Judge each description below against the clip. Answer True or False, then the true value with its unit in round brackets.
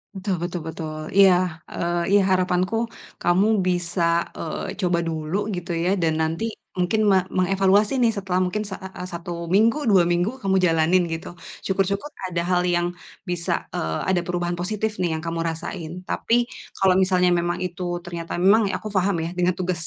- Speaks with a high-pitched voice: False (180 Hz)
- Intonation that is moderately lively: False (2.0 semitones)